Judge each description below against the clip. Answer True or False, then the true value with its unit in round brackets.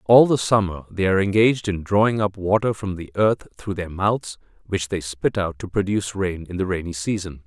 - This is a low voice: True (95 Hz)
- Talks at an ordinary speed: False (215 wpm)